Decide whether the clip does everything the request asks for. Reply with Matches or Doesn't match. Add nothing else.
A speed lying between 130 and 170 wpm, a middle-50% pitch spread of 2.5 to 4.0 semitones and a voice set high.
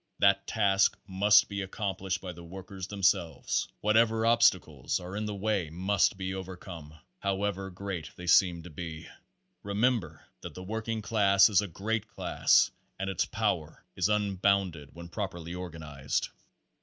Doesn't match